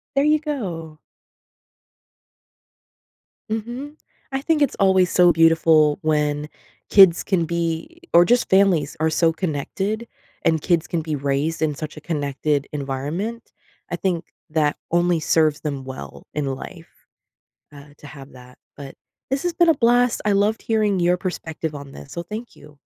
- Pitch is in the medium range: Yes, medium, 165 Hz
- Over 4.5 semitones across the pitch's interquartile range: Yes, wide, 5.6 semitones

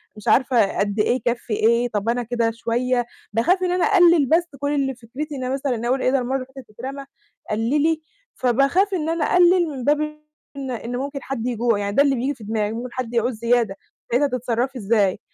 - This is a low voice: No, very high, 250 Hz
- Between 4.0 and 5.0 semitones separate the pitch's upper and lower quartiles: No, average, 3.5 semitones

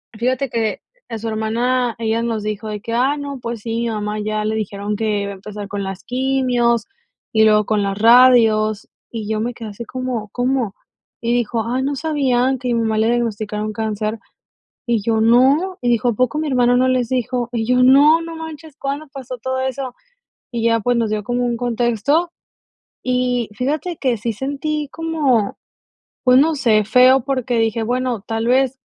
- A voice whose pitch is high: Yes, high, 240 Hz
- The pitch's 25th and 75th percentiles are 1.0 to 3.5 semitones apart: Yes, average, 2.9 semitones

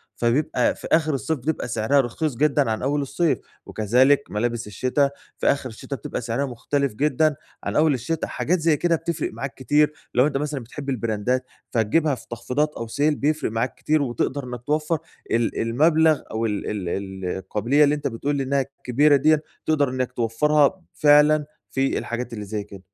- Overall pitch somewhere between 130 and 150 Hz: Yes, low, 135 Hz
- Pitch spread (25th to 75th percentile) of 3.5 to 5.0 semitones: Yes, average, 4.2 semitones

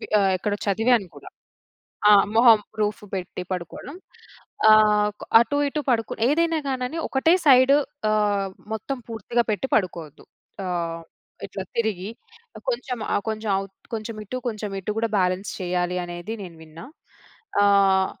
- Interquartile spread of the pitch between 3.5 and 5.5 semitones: Yes, average, 4.0 semitones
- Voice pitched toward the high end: Yes, high, 210 Hz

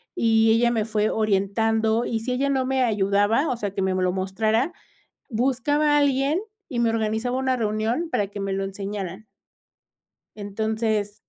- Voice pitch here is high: Yes, high, 220 Hz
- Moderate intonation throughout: Yes, average, 3.5 semitones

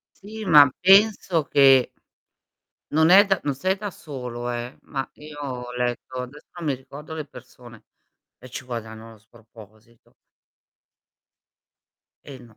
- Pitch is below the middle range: Yes, low, 130 Hz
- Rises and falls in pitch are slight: No, average, 4.5 semitones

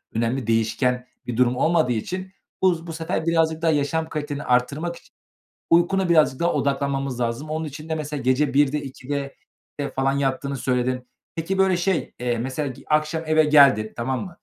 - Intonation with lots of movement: No, average, 4.0 semitones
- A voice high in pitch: No, medium, 145 Hz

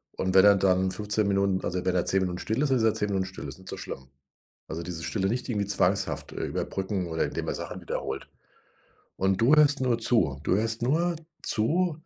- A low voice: Yes, low, 100 Hz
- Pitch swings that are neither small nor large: Yes, average, 3.7 semitones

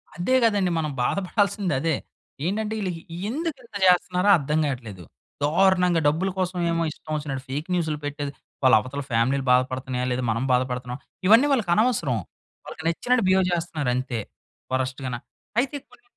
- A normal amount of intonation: No, wide, 6.5 semitones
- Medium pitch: Yes, medium, 160 Hz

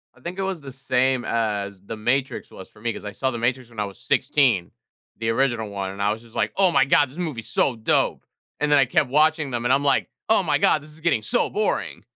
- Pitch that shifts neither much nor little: Yes, average, 4.6 semitones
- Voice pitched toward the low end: Yes, low, 130 Hz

